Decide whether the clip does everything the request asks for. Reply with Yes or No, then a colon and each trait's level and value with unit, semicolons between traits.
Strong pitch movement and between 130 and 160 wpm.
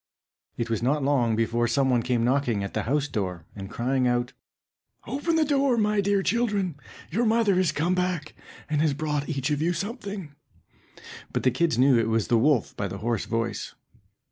No: wide, 7.8 semitones; average, 195 wpm